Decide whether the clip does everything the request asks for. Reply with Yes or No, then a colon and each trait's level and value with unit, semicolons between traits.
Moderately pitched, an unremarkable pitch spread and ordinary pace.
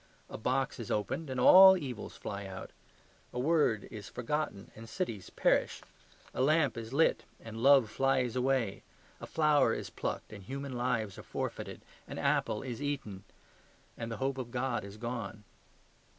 No: low, 125 Hz; average, 3.9 semitones; average, 165 wpm